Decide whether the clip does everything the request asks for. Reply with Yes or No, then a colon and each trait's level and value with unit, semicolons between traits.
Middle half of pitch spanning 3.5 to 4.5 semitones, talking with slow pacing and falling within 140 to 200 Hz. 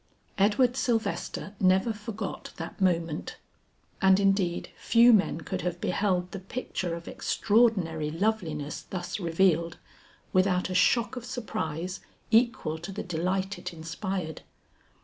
Yes: average, 3.8 semitones; slow, 125 wpm; medium, 185 Hz